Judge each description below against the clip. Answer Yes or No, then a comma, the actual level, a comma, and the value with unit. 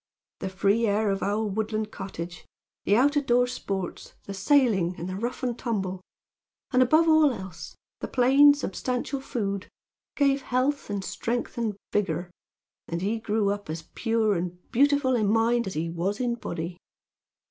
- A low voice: No, high, 215 Hz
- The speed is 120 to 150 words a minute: No, average, 165 wpm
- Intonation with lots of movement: No, average, 4.6 semitones